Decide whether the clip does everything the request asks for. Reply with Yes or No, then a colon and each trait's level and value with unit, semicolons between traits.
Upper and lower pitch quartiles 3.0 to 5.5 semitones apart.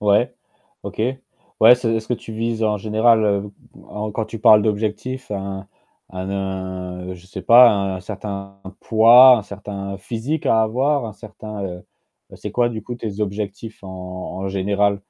No: narrow, 2.6 semitones